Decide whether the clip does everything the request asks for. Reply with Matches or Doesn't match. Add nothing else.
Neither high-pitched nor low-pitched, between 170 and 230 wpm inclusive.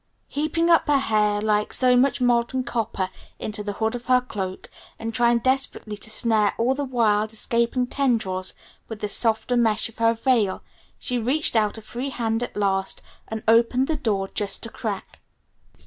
Doesn't match